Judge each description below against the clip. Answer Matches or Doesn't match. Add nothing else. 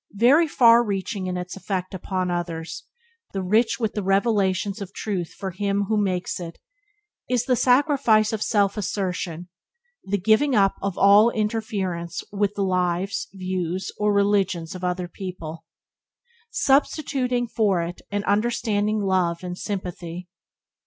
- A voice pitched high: Matches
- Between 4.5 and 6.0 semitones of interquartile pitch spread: Doesn't match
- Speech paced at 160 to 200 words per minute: Doesn't match